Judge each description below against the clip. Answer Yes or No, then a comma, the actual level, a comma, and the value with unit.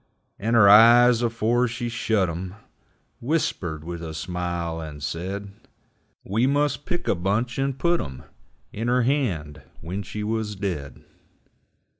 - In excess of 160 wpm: No, average, 140 wpm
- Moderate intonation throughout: No, wide, 5.8 semitones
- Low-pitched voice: Yes, low, 105 Hz